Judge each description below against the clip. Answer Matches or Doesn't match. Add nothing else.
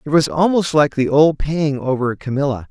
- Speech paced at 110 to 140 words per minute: Doesn't match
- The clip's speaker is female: Doesn't match